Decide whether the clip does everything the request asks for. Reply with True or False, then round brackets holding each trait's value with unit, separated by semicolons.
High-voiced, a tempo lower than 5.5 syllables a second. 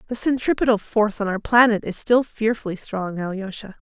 False (215 Hz; 5.6 syllables/s)